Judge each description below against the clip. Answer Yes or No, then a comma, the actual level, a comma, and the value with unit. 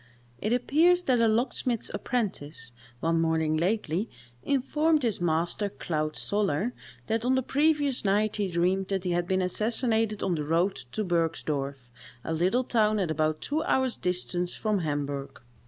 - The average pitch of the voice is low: No, high, 195 Hz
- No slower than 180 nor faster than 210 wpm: No, average, 155 wpm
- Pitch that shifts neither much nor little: No, wide, 6.2 semitones